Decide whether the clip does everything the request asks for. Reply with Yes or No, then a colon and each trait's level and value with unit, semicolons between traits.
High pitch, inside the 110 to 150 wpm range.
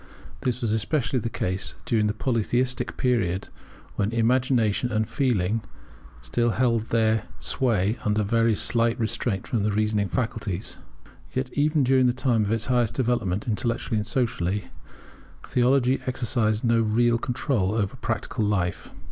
No: low, 115 Hz; average, 140 wpm